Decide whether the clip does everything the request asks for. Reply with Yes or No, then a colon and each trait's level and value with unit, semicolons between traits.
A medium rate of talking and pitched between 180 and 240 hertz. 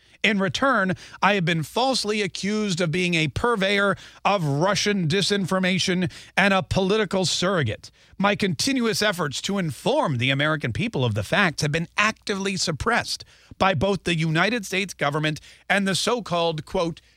Yes: average, 155 wpm; high, 190 Hz